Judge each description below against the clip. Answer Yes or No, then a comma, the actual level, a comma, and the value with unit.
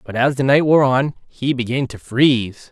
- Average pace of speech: No, fast, 220 wpm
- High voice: No, low, 130 Hz